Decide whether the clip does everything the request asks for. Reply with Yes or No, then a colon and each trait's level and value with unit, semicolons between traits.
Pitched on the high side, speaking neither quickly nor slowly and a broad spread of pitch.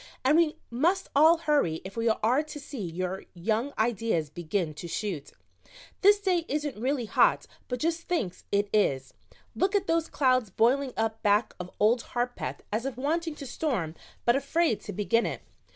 Yes: high, 240 Hz; average, 175 wpm; wide, 6.7 semitones